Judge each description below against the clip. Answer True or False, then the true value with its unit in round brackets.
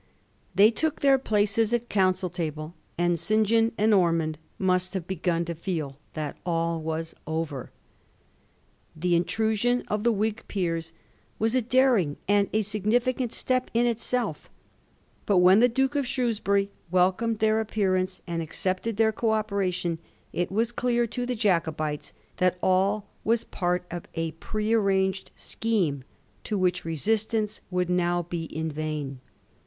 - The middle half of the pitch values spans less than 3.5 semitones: False (4.7 semitones)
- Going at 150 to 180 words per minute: True (155 wpm)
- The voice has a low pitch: False (195 Hz)